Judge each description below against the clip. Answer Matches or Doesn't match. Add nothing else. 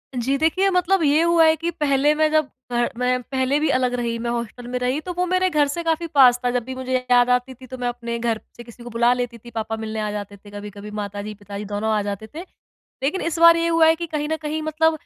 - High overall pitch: Matches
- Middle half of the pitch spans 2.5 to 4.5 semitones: Doesn't match